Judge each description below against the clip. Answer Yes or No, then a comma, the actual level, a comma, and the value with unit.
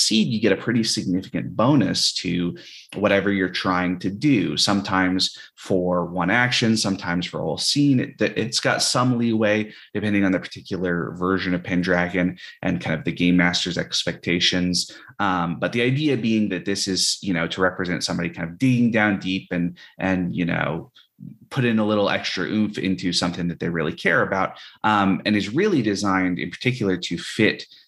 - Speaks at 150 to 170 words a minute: No, average, 185 wpm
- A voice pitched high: No, very low, 95 Hz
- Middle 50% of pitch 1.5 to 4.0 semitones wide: Yes, average, 2.9 semitones